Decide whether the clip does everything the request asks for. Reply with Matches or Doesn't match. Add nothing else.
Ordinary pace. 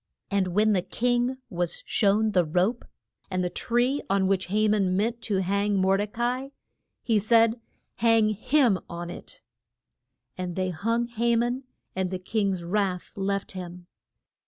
Matches